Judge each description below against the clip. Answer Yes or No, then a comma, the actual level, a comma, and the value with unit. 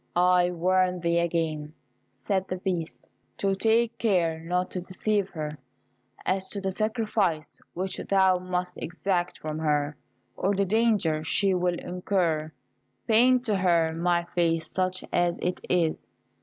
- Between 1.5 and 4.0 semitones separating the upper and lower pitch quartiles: Yes, narrow, 2.6 semitones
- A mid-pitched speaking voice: Yes, medium, 180 Hz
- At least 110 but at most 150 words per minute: Yes, average, 140 wpm